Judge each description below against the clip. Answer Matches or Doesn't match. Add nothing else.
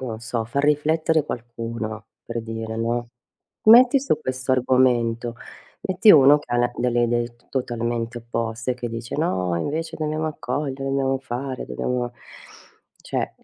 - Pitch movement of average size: Matches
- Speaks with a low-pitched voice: Matches